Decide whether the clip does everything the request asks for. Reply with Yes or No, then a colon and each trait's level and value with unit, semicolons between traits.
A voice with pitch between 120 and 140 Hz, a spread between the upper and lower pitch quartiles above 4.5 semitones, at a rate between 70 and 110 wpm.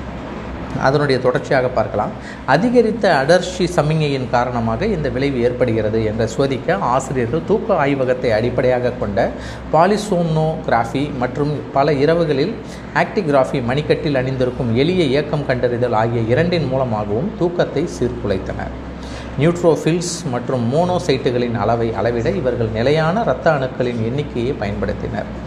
Yes: low, 135 Hz; average, 5.1 semitones; average, 100 wpm